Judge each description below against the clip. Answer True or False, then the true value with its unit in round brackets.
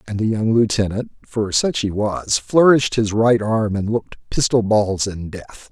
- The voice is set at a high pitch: False (105 Hz)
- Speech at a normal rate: True (190 wpm)